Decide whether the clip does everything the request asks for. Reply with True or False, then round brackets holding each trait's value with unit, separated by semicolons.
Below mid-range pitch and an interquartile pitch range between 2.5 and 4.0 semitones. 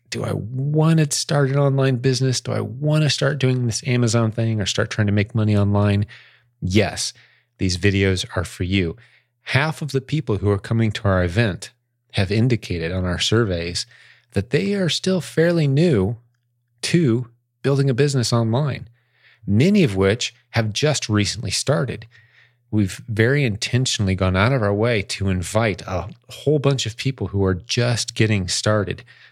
False (115 Hz; 4.7 semitones)